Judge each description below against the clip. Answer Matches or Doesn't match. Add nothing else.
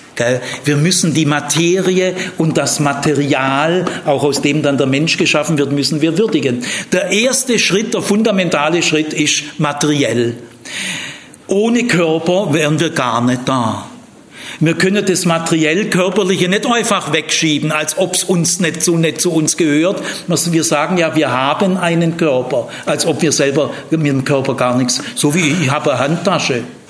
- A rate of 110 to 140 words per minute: Doesn't match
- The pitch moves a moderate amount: Matches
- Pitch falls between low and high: Matches